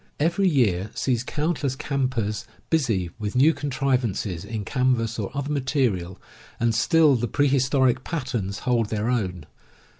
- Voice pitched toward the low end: Yes, low, 125 Hz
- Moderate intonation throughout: Yes, average, 4.6 semitones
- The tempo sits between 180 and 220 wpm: No, average, 145 wpm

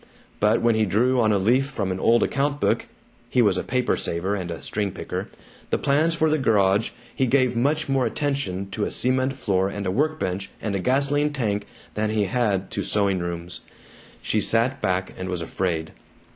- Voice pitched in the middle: No, low, 110 Hz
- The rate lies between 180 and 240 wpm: Yes, average, 200 wpm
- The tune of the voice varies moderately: No, wide, 5.7 semitones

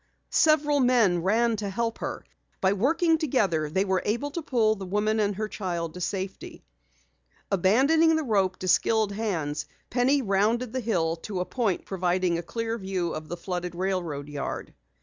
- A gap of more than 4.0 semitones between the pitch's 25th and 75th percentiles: Yes, average, 4.6 semitones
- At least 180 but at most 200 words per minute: No, average, 170 wpm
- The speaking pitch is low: No, high, 200 Hz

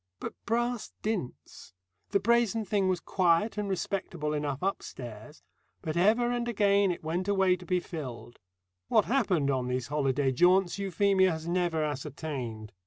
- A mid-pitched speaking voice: Yes, medium, 180 Hz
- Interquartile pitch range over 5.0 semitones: Yes, wide, 5.4 semitones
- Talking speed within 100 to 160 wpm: Yes, average, 150 wpm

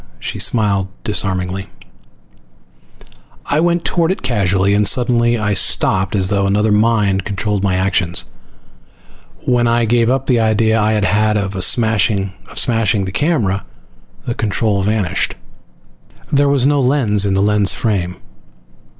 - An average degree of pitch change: Yes, average, 3.2 semitones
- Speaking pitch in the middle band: No, low, 105 Hz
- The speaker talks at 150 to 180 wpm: No, slow, 135 wpm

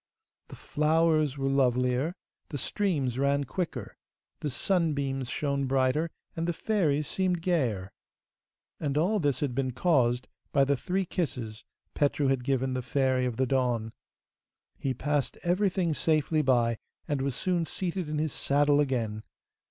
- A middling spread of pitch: Yes, average, 3.9 semitones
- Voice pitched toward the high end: No, medium, 140 Hz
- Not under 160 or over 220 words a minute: No, average, 145 wpm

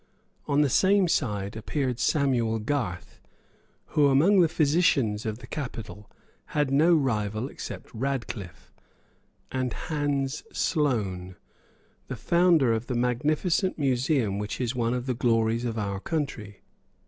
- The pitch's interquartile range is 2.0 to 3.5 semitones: No, average, 4.8 semitones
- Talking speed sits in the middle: No, slow, 130 wpm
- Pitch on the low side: Yes, low, 125 Hz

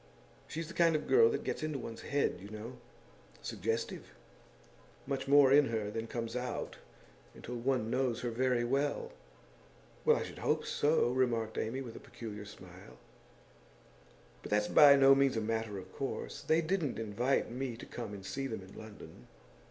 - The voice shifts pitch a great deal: No, average, 3.6 semitones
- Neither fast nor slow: Yes, average, 175 wpm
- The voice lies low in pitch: Yes, low, 125 Hz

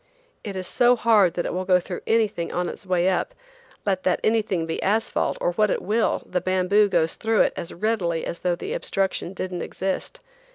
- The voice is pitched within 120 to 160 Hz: No, high, 190 Hz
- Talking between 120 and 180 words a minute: No, fast, 205 wpm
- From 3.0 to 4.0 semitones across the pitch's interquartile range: Yes, average, 3.3 semitones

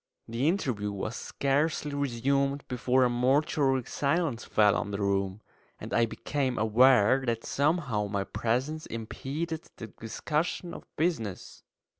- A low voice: Yes, low, 130 Hz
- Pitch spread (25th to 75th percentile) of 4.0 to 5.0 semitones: Yes, average, 4.5 semitones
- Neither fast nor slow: No, slow, 130 wpm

